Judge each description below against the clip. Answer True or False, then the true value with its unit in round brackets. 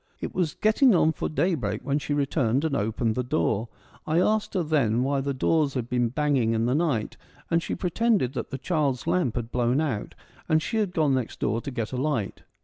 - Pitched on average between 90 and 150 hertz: True (140 Hz)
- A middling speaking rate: False (225 wpm)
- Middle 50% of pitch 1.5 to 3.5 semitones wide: False (4.9 semitones)